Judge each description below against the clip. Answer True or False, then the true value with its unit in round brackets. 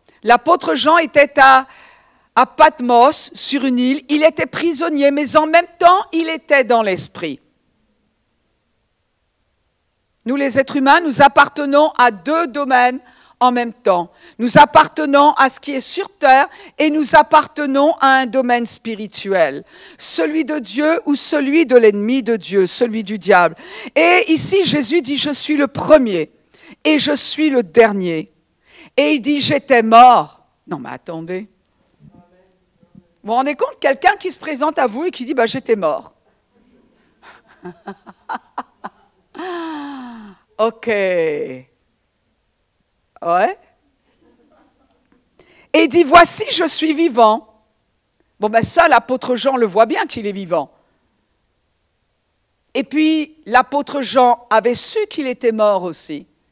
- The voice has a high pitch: True (265 Hz)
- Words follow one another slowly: True (135 wpm)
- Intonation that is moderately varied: False (6.3 semitones)